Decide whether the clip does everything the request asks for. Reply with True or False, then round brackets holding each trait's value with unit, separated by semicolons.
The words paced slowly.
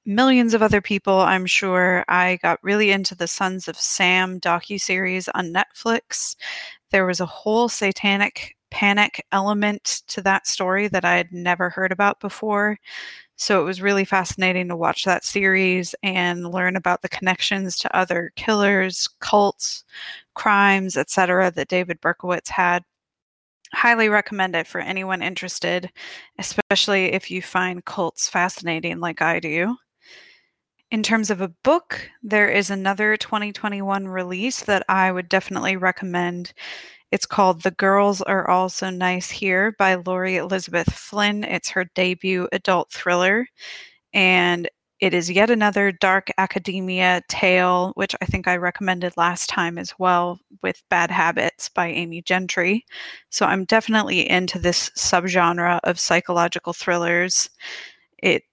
False (145 wpm)